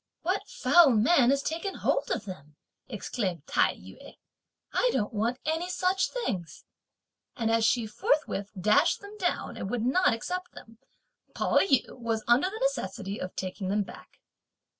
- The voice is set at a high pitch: Yes, high, 240 Hz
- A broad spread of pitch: Yes, wide, 9.0 semitones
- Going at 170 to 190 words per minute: No, average, 160 wpm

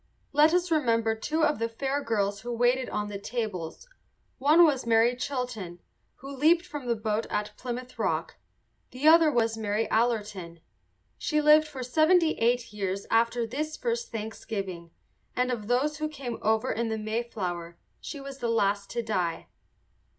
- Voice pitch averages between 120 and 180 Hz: No, high, 235 Hz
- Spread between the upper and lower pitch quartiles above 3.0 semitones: Yes, average, 4.9 semitones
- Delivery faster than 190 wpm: No, average, 165 wpm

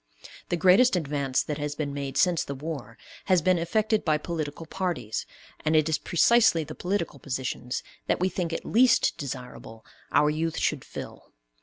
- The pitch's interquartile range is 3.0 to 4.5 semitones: Yes, average, 4.2 semitones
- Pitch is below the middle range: No, medium, 155 Hz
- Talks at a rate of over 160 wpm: Yes, average, 170 wpm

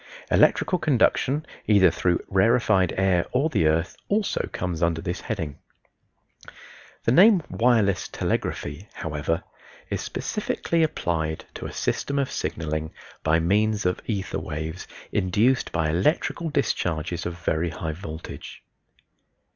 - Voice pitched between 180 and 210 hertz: No, very low, 90 Hz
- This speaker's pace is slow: Yes, slow, 125 wpm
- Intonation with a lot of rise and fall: Yes, wide, 6.4 semitones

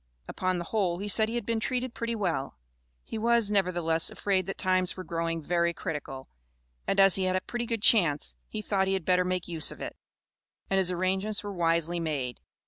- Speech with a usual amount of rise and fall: Yes, average, 3.5 semitones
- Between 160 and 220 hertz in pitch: Yes, medium, 185 Hz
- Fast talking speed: Yes, fast, 210 wpm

